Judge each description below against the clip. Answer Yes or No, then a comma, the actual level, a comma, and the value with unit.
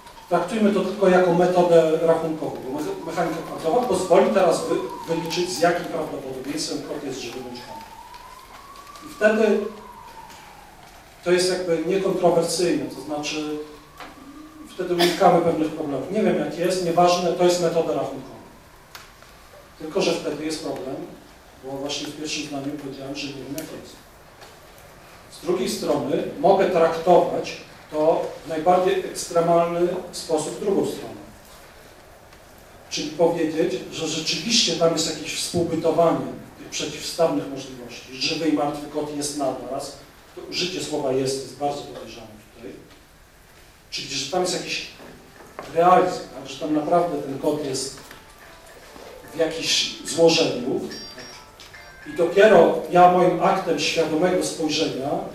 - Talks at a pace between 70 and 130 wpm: Yes, average, 125 wpm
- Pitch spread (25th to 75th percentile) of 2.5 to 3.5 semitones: Yes, average, 2.9 semitones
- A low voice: No, medium, 165 Hz